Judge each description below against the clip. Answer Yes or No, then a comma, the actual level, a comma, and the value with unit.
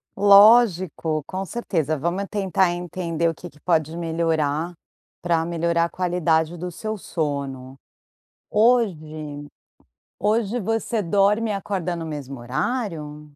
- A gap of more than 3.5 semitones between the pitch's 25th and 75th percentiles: Yes, average, 4.1 semitones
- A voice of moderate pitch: Yes, medium, 170 Hz